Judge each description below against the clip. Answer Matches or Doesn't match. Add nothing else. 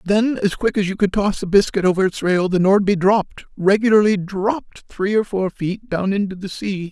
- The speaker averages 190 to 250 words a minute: Matches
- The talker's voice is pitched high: Matches